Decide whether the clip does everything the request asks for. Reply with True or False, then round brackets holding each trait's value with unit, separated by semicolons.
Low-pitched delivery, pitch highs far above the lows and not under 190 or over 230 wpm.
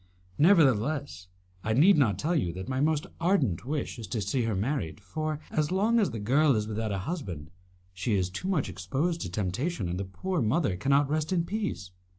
True (130 Hz; 8.2 semitones; 200 wpm)